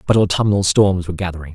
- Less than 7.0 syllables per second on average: No, 7.1 syllables/s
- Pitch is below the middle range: Yes, very low, 95 Hz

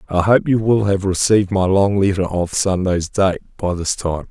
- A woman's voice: No, male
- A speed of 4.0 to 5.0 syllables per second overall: Yes, 4.9 syllables/s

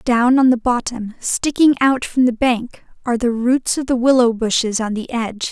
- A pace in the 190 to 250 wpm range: Yes, fast, 205 wpm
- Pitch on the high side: Yes, high, 240 Hz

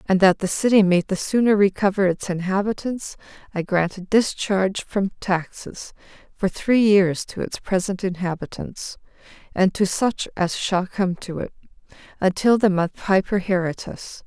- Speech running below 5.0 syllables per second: Yes, 4.6 syllables/s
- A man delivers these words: No, female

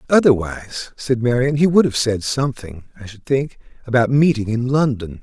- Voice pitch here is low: Yes, low, 125 Hz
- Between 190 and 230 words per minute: No, average, 170 wpm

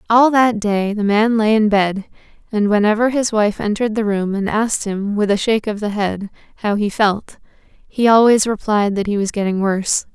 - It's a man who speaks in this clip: No, female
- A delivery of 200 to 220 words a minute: Yes, fast, 205 wpm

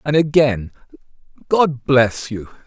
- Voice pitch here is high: No, low, 135 Hz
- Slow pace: Yes, slow, 110 wpm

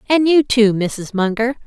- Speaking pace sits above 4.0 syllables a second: Yes, 4.4 syllables/s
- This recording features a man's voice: No, female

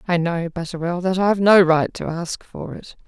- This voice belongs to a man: No, female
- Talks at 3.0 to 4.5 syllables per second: No, 4.9 syllables/s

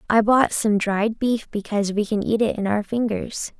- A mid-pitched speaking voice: No, high, 215 Hz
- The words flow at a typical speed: No, fast, 215 wpm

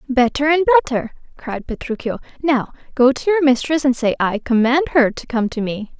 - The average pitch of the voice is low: No, very high, 260 Hz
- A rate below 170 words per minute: No, average, 190 wpm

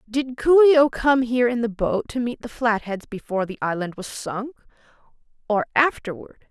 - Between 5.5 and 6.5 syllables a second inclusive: No, 5.3 syllables/s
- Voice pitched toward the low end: No, high, 235 Hz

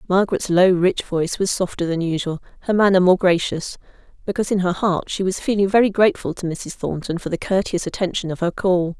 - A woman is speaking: Yes, female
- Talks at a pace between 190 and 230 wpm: Yes, fast, 205 wpm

